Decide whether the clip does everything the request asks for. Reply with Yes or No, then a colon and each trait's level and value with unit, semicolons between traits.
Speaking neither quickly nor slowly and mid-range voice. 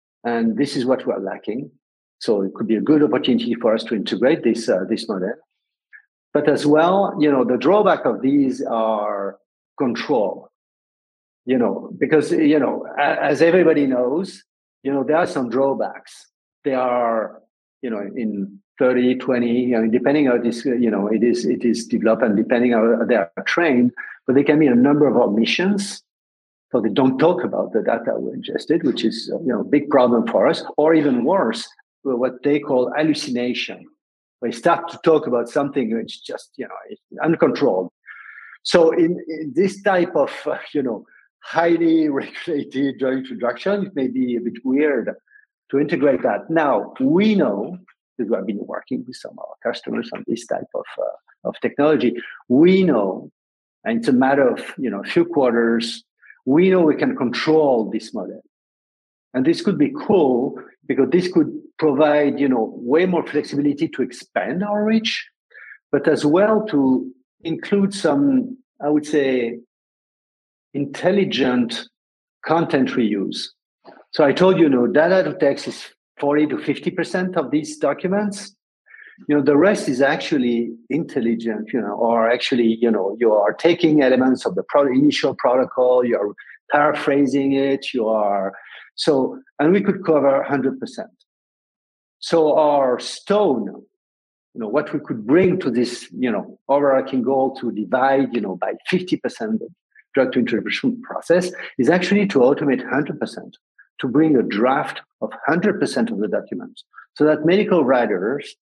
Yes: average, 170 wpm; medium, 145 Hz